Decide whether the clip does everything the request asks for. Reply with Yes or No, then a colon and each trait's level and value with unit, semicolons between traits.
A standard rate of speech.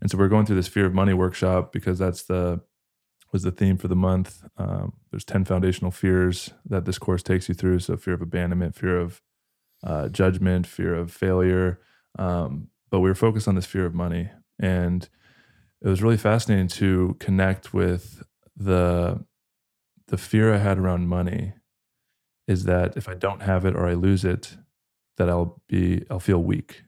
Yes: average, 185 wpm